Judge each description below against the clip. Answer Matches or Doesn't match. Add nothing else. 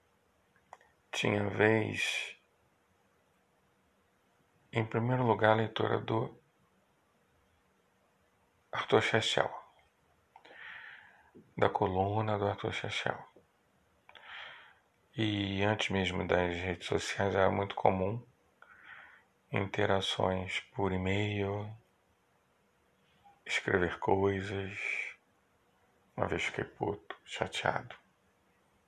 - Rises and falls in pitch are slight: Matches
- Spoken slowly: Matches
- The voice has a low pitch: Matches